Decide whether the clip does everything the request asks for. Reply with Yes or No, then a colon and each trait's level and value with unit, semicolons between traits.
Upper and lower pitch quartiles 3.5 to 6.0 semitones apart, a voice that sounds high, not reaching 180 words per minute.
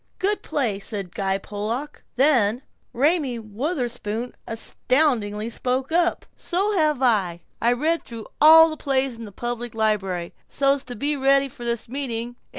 Yes: average, 4.6 semitones; high, 245 Hz; average, 150 wpm